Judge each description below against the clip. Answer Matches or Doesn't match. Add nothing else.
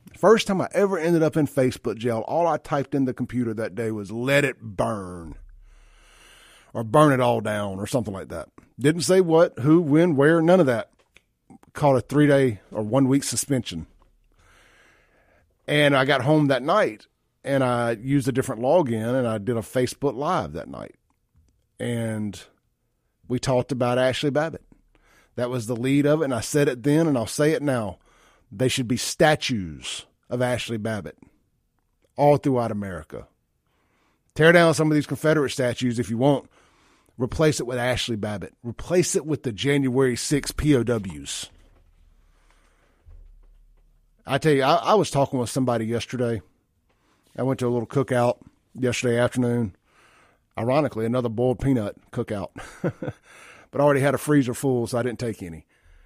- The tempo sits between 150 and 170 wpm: Matches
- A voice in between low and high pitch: Doesn't match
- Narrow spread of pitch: Doesn't match